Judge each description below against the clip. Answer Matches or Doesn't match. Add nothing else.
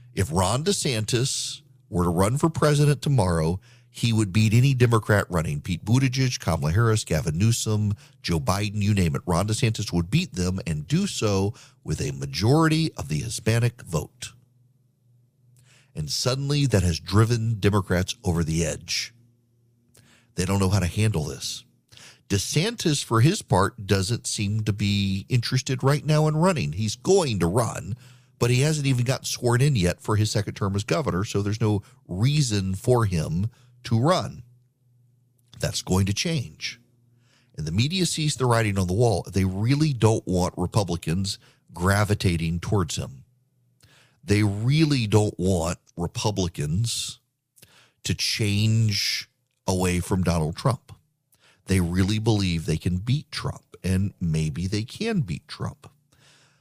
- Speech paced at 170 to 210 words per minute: Doesn't match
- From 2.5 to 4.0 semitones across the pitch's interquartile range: Doesn't match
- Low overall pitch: Matches